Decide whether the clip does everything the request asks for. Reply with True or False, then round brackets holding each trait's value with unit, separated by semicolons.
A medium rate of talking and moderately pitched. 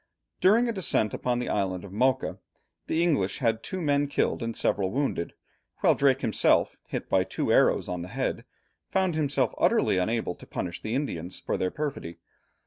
False (180 wpm; 125 Hz)